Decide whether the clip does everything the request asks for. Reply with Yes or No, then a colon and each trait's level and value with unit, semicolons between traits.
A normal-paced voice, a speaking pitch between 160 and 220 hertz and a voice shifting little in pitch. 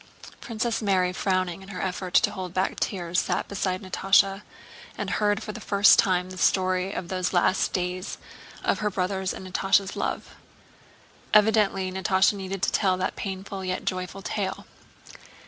Yes: average, 165 wpm; high, 190 Hz; narrow, 1.2 semitones